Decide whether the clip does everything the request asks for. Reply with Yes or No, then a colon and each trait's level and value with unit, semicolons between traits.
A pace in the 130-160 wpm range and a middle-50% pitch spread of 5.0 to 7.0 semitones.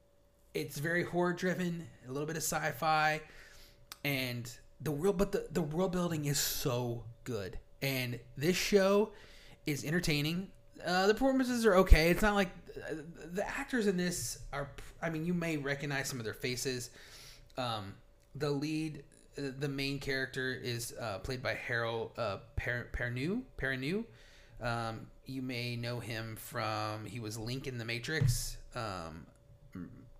Yes: average, 150 wpm; wide, 5.6 semitones